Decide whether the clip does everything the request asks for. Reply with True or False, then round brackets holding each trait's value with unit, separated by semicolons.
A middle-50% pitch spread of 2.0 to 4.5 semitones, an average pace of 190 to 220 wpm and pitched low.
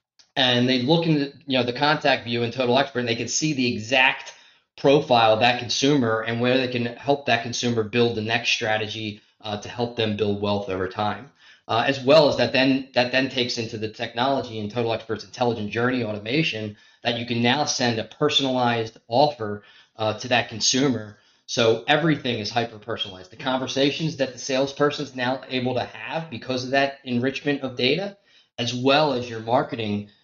True (3.1 semitones; 195 wpm; 120 Hz)